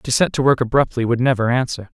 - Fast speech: Yes, fast, 240 wpm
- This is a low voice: Yes, low, 125 Hz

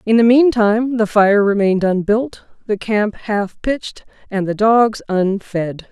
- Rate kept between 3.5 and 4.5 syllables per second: Yes, 4.2 syllables/s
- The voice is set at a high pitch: Yes, high, 210 Hz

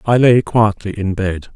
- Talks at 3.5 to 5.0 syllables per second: Yes, 4.3 syllables/s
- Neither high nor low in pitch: No, low, 105 Hz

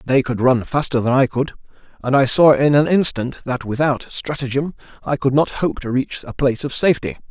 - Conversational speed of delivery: No, fast, 215 wpm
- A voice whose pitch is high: No, low, 135 Hz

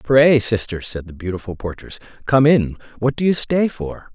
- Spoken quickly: No, average, 190 wpm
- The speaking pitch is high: No, low, 115 Hz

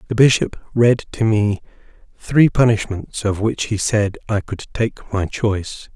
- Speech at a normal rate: Yes, average, 160 wpm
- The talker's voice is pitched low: Yes, low, 110 Hz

